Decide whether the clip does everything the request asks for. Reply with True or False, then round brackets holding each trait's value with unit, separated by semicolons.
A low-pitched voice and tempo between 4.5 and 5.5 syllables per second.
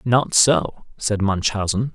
False (100 Hz; 3.5 syllables/s)